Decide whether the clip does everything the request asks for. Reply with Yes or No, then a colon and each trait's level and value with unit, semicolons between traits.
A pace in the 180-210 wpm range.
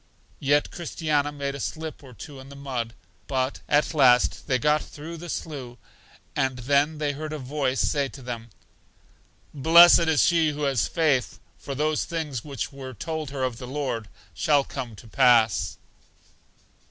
No: average, 165 wpm